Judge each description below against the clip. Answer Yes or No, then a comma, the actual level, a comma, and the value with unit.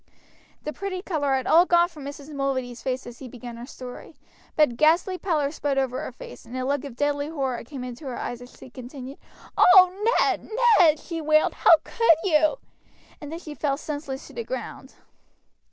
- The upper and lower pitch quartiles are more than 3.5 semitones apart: Yes, average, 4.1 semitones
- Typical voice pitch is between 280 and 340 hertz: Yes, very high, 285 Hz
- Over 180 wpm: Yes, average, 200 wpm